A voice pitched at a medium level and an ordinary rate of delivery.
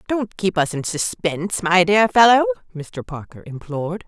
Yes: medium, 175 Hz; average, 160 wpm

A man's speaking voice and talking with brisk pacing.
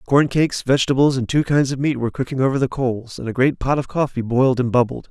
Yes: male; fast, 260 wpm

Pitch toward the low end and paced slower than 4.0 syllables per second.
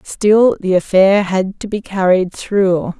No: high, 195 Hz; 3.6 syllables/s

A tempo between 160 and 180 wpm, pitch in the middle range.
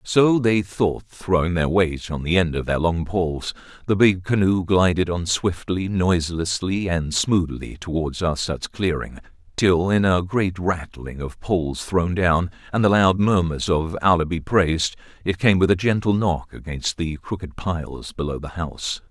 No: average, 175 wpm; very low, 90 Hz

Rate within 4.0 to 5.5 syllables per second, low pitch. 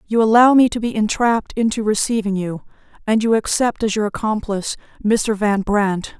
No: 5.2 syllables/s; high, 215 Hz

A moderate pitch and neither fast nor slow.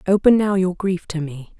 No: medium, 180 Hz; fast, 225 wpm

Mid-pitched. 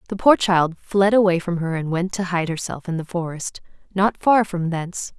Yes: medium, 180 Hz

